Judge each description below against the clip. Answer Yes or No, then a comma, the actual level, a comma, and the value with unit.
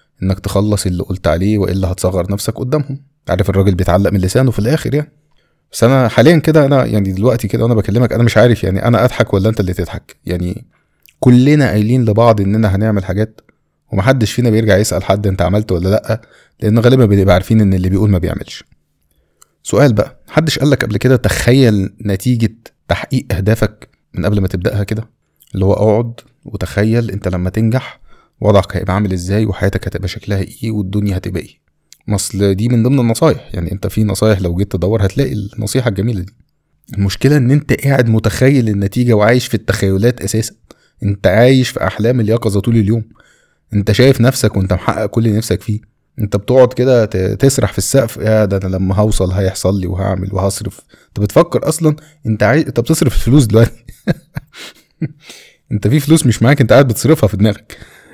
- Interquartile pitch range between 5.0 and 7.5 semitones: No, average, 3.9 semitones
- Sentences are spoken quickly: Yes, fast, 175 wpm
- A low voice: Yes, low, 110 Hz